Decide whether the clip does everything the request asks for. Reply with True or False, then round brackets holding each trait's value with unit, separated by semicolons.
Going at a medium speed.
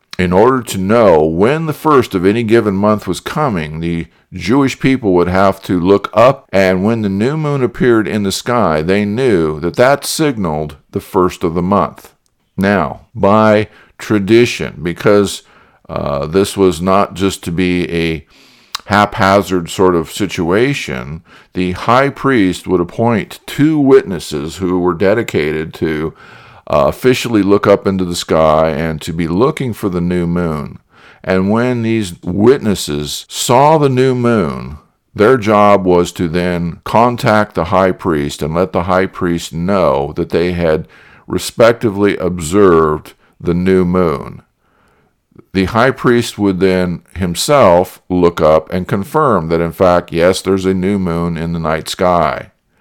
True (155 wpm)